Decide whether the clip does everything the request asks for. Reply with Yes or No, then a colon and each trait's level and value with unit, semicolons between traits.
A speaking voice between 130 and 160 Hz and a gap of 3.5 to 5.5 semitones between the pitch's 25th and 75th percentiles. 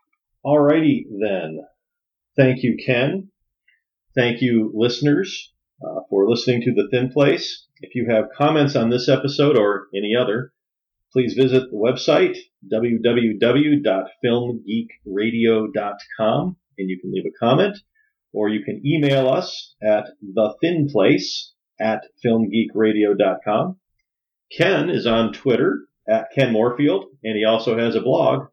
No: low, 120 Hz; average, 4.8 semitones